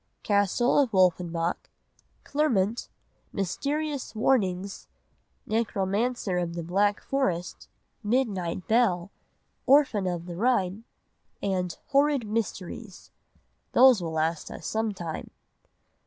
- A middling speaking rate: No, slow, 95 wpm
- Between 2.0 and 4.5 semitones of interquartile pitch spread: No, average, 5.2 semitones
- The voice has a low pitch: No, high, 200 Hz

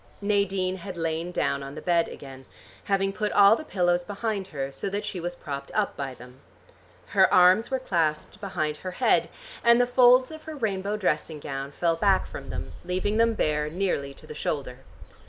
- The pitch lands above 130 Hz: Yes, medium, 185 Hz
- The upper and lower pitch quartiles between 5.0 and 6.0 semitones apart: Yes, average, 5.3 semitones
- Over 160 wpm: Yes, average, 190 wpm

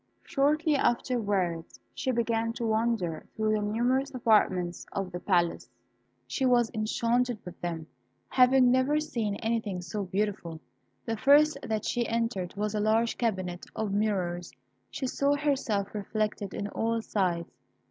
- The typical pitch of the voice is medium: No, high, 220 Hz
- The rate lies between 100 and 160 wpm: Yes, average, 140 wpm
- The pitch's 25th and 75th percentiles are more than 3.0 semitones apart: Yes, average, 4.0 semitones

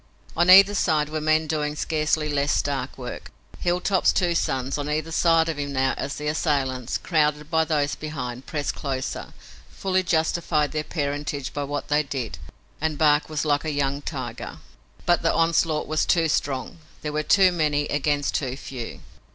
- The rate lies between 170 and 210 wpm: Yes, average, 175 wpm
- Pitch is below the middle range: No, medium, 150 Hz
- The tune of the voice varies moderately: No, narrow, 2.1 semitones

